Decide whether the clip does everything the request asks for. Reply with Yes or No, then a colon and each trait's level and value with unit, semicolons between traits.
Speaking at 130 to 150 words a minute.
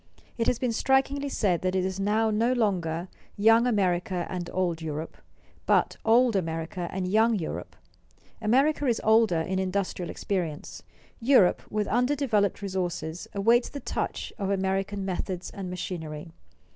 Yes: average, 145 wpm